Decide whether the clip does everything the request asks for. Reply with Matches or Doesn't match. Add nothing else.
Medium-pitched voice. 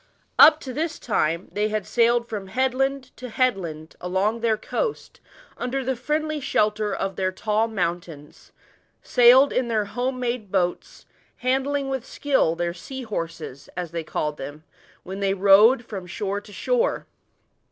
Doesn't match